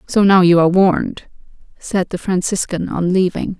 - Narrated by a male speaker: No, female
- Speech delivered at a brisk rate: No, average, 165 wpm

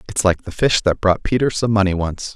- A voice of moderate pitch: No, low, 100 Hz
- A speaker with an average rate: No, fast, 255 wpm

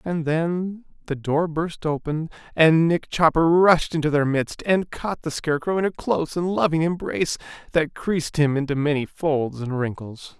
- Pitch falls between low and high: Yes, medium, 160 Hz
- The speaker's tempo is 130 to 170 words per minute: No, average, 180 wpm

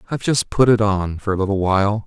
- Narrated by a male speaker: Yes, male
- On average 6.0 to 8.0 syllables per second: Yes, 6.5 syllables/s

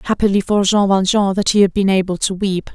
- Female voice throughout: Yes, female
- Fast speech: Yes, fast, 240 wpm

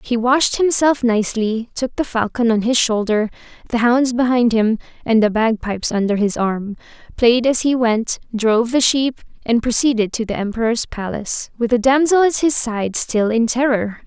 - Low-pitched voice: No, high, 235 Hz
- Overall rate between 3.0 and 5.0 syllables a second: Yes, 4.8 syllables/s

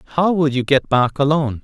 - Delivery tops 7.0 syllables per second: No, 6.2 syllables/s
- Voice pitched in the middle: Yes, medium, 145 Hz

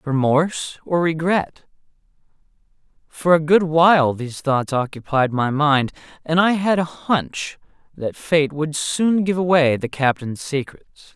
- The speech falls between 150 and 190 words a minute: No, average, 140 wpm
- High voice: No, medium, 155 Hz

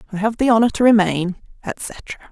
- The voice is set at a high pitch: Yes, high, 215 Hz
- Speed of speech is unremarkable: Yes, average, 180 wpm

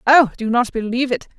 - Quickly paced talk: Yes, fast, 215 wpm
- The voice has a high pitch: Yes, high, 245 Hz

